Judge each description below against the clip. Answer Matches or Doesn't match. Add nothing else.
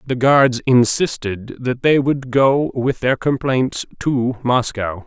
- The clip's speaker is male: Matches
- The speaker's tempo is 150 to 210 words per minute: Doesn't match